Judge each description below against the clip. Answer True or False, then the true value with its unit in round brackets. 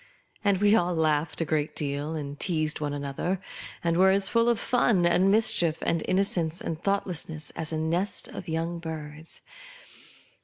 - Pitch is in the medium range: True (165 Hz)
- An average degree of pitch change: True (3.5 semitones)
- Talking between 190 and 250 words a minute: False (165 wpm)